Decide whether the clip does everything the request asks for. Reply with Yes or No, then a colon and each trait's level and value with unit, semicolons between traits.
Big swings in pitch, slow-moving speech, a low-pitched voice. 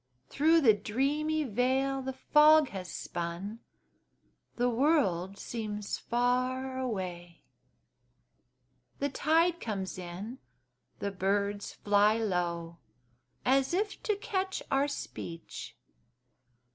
No: wide, 6.3 semitones; slow, 95 wpm; high, 240 Hz